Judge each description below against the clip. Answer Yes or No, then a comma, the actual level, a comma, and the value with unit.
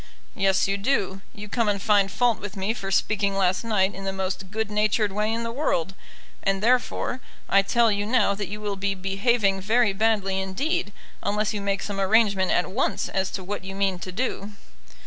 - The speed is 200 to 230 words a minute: Yes, fast, 205 wpm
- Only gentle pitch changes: Yes, narrow, 2.1 semitones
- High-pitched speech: Yes, high, 200 Hz